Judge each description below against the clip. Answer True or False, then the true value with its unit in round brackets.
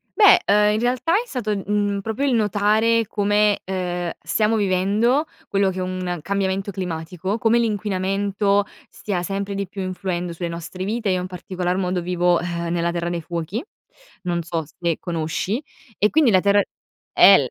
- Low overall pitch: False (195 Hz)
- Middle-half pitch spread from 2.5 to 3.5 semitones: True (2.8 semitones)